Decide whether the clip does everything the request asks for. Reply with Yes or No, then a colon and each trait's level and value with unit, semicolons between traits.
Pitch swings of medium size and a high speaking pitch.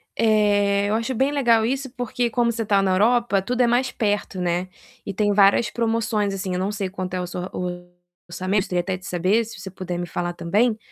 Yes: average, 3.7 semitones; high, 205 Hz